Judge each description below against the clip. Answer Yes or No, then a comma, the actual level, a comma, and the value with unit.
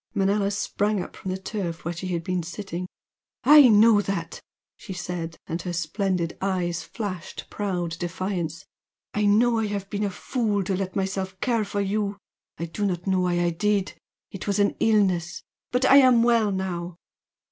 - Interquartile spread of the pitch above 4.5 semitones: No, average, 2.8 semitones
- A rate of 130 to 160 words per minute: No, average, 180 wpm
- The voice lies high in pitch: Yes, high, 195 Hz